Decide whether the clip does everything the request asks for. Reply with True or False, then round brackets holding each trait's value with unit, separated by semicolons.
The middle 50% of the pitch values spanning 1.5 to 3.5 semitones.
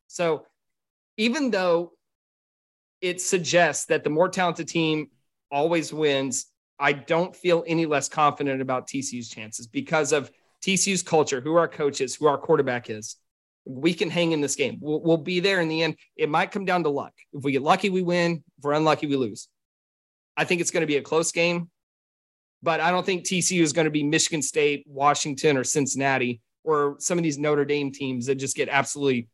False (3.9 semitones)